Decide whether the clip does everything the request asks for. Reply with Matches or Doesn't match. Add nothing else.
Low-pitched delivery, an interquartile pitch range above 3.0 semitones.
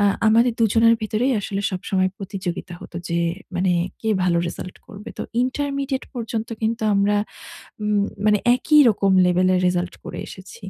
Doesn't match